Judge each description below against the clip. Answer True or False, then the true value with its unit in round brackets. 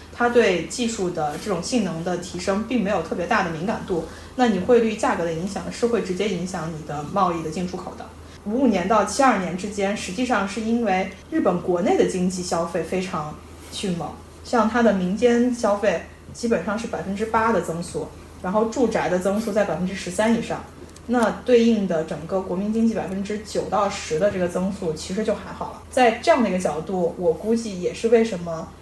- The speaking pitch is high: True (200 Hz)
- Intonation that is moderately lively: True (4.1 semitones)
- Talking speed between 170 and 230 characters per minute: False (310 characters per minute)